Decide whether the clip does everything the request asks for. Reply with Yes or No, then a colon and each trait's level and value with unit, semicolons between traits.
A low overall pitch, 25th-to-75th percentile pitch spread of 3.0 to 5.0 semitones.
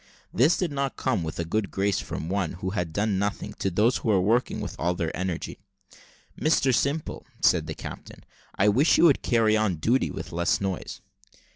No: low, 100 Hz; wide, 5.4 semitones